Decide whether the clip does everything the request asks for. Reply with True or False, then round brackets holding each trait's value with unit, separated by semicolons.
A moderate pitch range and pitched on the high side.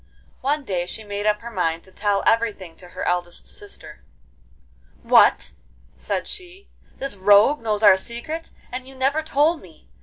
False (6.8 semitones; 205 Hz)